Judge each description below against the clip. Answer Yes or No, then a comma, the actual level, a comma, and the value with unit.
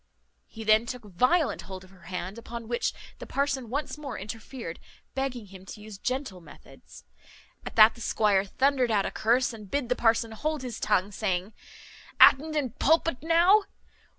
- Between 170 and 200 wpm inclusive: Yes, average, 175 wpm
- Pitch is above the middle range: Yes, high, 230 Hz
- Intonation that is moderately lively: Yes, average, 4.8 semitones